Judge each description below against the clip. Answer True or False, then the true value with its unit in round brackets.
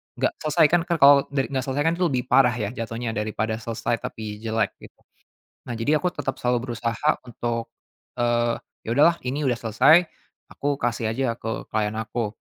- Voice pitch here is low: True (120 Hz)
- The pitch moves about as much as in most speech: True (3.6 semitones)